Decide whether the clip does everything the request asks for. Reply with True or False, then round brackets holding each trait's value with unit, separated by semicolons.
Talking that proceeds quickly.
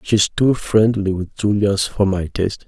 False (180 wpm)